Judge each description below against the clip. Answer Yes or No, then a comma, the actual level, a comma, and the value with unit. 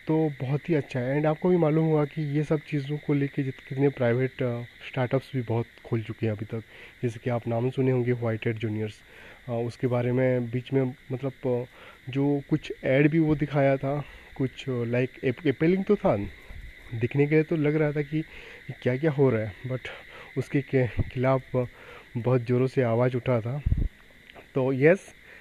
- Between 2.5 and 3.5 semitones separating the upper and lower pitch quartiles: Yes, average, 3.0 semitones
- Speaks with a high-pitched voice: No, low, 130 Hz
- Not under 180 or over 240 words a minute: Yes, average, 185 wpm